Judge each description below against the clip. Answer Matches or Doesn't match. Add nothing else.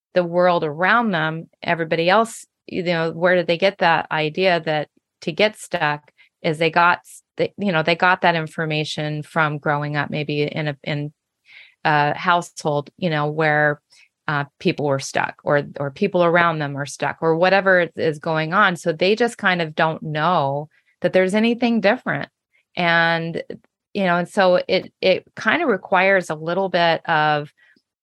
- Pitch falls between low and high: Matches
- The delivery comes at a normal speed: Matches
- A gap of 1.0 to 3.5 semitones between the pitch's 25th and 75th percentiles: Matches